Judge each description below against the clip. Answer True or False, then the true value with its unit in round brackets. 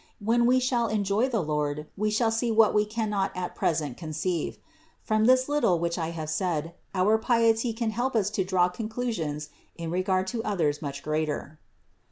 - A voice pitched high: True (195 Hz)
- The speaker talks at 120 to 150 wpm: False (180 wpm)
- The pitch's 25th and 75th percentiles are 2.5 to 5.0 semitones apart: False (5.6 semitones)